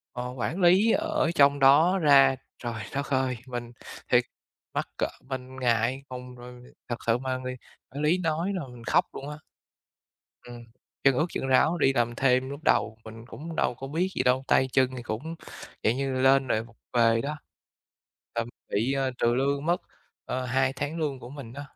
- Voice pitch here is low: Yes, low, 130 Hz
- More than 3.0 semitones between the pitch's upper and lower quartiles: No, average, 2.7 semitones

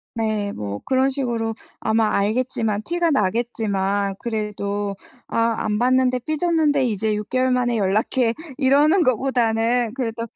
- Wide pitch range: No, average, 3.6 semitones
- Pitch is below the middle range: No, high, 230 Hz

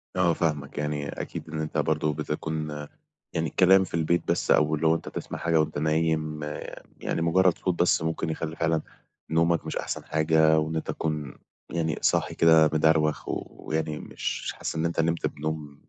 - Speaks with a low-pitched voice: Yes, very low, 80 Hz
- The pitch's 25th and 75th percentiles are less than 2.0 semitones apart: Yes, narrow, 1.1 semitones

